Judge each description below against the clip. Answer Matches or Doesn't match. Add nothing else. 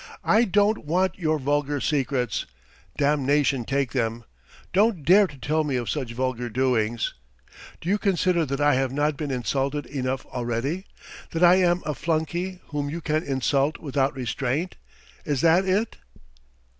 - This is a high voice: Doesn't match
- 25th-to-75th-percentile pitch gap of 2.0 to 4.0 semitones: Doesn't match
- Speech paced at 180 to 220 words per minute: Doesn't match